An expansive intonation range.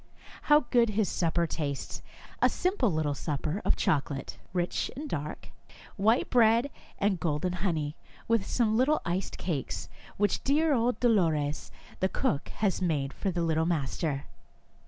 Yes: wide, 6.7 semitones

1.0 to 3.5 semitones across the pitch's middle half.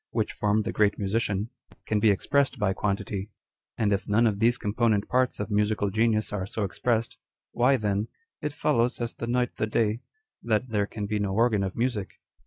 Yes: narrow, 2.4 semitones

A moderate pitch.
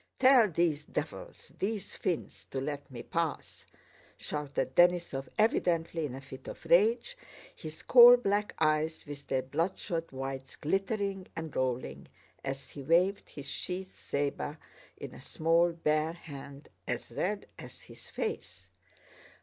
Yes: medium, 165 Hz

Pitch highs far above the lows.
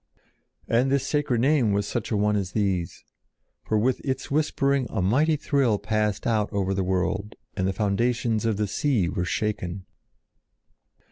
No: average, 4.6 semitones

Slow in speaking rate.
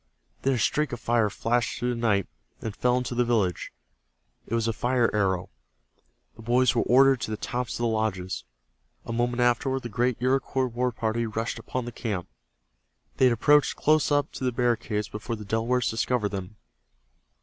No: average, 185 wpm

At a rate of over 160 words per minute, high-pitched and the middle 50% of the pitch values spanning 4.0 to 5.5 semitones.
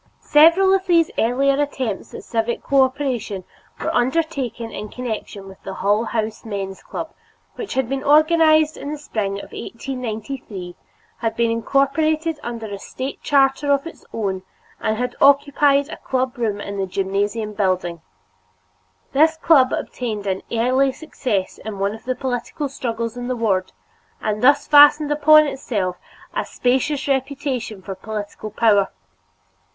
No: average, 145 wpm; high, 245 Hz; average, 5.1 semitones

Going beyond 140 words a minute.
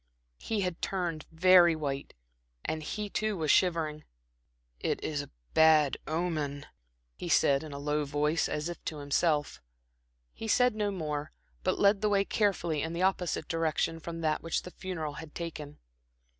Yes: average, 165 wpm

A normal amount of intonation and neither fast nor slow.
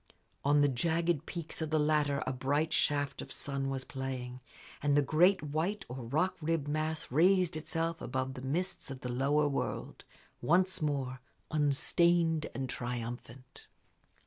Yes: average, 3.5 semitones; average, 150 wpm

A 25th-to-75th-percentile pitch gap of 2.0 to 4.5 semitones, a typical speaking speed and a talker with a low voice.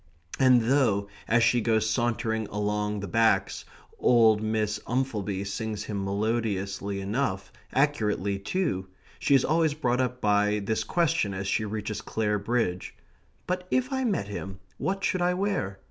Yes: average, 4.2 semitones; average, 150 wpm; low, 110 Hz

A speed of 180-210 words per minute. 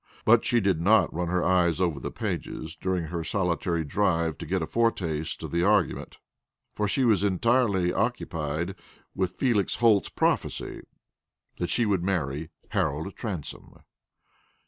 No: average, 145 wpm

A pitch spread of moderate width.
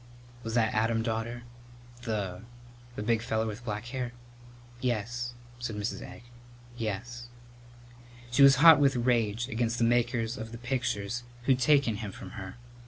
No: narrow, 1.8 semitones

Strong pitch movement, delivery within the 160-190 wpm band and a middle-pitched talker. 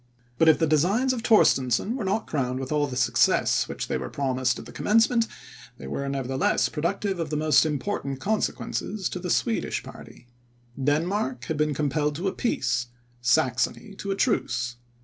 Yes: wide, 7.2 semitones; average, 175 wpm; medium, 155 Hz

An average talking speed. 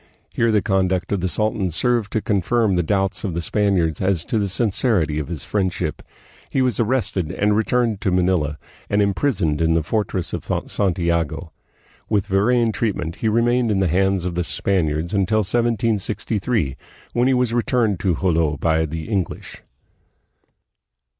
Yes: average, 160 wpm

